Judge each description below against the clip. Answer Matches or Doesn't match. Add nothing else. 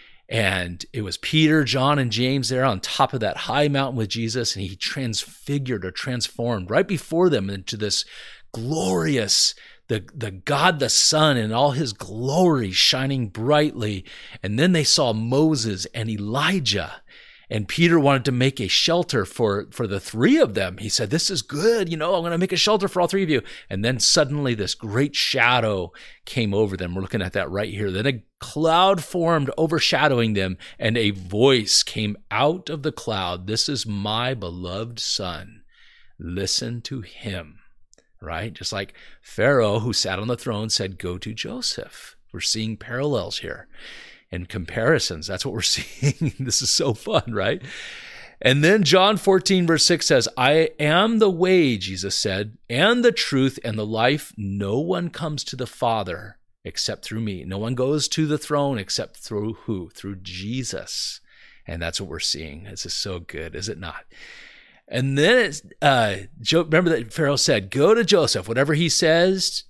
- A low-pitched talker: Matches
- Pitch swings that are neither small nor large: Doesn't match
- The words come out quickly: Doesn't match